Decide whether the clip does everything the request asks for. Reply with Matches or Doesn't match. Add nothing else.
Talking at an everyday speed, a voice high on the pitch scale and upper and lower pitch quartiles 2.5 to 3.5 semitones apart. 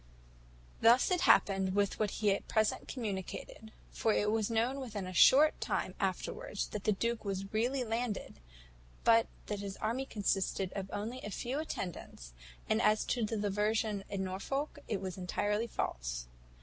Matches